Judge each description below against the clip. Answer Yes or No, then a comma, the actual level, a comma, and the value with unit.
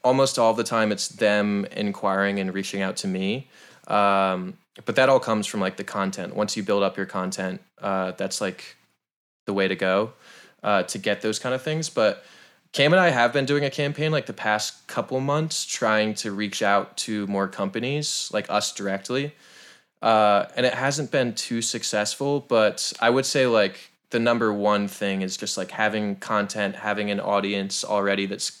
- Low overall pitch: Yes, low, 105 Hz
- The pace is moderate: Yes, average, 190 wpm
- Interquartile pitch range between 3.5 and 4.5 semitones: Yes, average, 3.9 semitones